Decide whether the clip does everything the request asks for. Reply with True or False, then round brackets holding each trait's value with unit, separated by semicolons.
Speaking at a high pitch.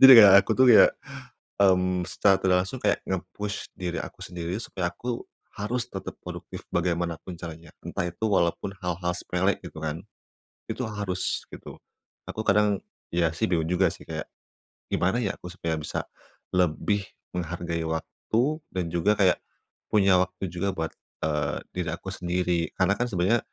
False (90 Hz)